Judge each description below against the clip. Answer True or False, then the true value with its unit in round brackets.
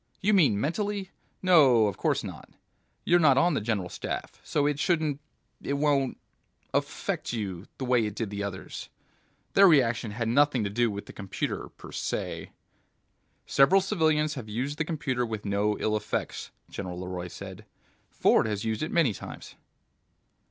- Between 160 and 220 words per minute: True (165 wpm)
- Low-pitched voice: True (125 Hz)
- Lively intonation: True (6.5 semitones)